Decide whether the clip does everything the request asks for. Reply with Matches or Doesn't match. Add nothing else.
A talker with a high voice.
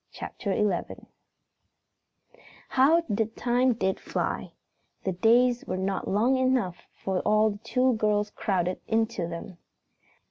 Matches